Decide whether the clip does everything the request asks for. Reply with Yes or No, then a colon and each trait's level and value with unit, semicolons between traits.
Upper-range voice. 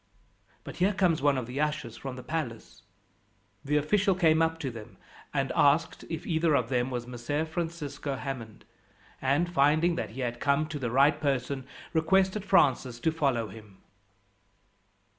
No: medium, 145 Hz